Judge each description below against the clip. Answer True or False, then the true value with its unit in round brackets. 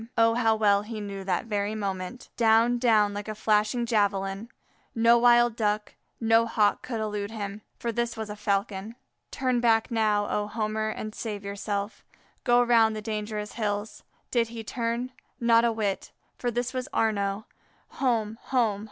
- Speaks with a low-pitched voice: False (220 Hz)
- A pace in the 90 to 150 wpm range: False (165 wpm)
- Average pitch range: False (2.1 semitones)